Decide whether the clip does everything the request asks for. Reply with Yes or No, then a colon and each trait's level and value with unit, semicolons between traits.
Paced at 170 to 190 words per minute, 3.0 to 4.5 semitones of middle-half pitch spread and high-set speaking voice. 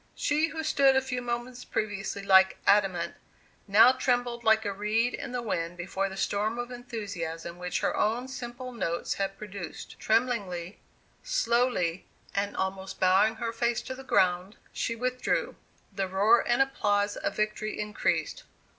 No: average, 155 wpm; average, 4.0 semitones; high, 215 Hz